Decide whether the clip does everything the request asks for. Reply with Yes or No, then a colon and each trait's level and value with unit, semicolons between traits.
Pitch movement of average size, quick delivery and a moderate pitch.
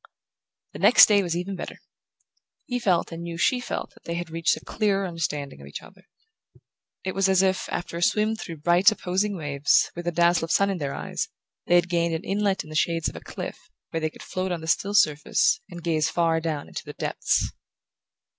Yes: average, 3.0 semitones; fast, 220 wpm; medium, 175 Hz